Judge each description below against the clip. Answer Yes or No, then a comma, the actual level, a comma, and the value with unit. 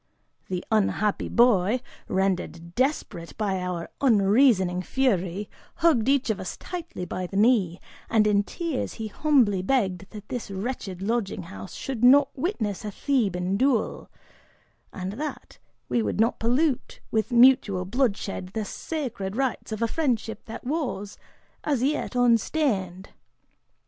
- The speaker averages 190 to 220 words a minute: No, slow, 135 wpm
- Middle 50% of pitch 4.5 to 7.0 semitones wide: Yes, average, 5.2 semitones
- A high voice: Yes, high, 220 Hz